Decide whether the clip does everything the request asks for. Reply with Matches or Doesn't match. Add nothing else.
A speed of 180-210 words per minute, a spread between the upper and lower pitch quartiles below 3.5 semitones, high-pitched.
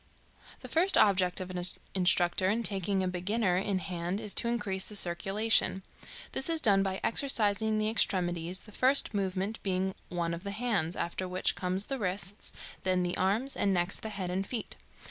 Matches